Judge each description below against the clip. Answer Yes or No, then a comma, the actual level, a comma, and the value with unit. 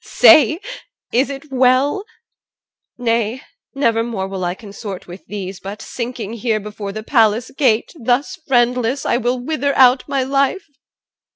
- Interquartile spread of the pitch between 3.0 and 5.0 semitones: Yes, average, 3.9 semitones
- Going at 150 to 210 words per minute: No, slow, 135 wpm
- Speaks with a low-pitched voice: No, high, 240 Hz